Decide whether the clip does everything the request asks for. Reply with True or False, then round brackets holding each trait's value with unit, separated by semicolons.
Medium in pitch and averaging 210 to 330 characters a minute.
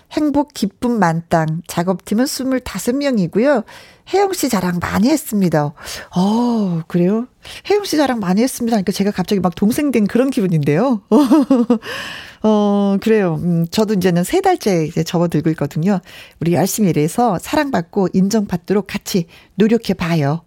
False (205 Hz; 310 characters per minute)